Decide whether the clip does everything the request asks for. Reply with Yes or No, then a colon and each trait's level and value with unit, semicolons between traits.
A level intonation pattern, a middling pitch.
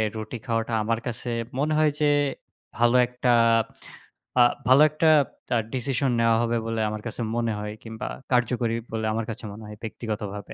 No: narrow, 2.0 semitones; low, 115 Hz